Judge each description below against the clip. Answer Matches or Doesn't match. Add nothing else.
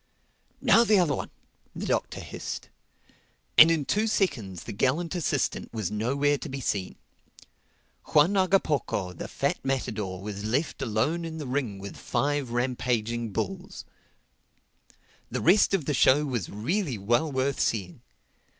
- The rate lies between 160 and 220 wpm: Doesn't match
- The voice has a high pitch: Doesn't match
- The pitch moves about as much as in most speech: Doesn't match